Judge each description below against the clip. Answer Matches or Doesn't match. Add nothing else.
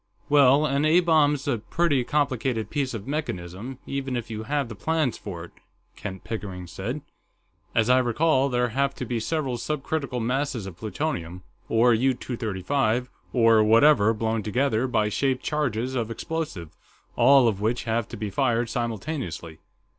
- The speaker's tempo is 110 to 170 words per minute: Matches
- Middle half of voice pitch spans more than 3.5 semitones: Matches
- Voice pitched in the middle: Doesn't match